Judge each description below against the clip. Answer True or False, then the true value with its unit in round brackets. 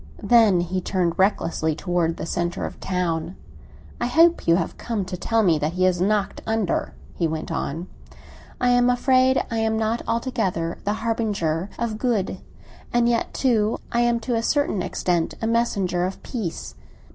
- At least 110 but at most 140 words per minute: False (175 wpm)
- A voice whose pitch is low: False (210 Hz)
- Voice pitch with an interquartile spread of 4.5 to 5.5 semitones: True (4.9 semitones)